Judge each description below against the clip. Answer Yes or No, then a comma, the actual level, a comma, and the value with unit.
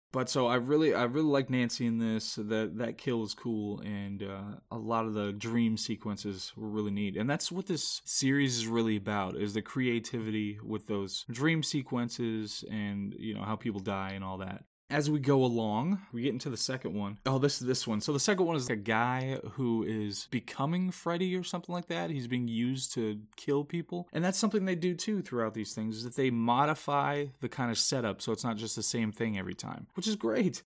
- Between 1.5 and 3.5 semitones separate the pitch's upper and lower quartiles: No, average, 4.7 semitones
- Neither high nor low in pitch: No, low, 120 Hz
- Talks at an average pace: No, fast, 225 wpm